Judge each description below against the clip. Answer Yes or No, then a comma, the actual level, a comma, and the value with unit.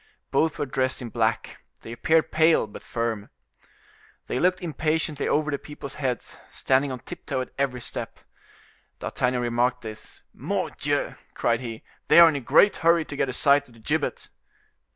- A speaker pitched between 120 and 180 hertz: Yes, low, 135 Hz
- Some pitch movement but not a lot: Yes, average, 4.2 semitones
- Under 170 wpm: No, average, 175 wpm